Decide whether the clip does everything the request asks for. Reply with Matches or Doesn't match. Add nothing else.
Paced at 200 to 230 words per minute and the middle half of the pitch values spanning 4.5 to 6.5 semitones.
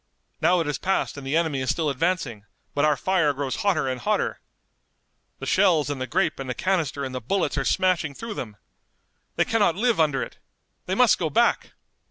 Matches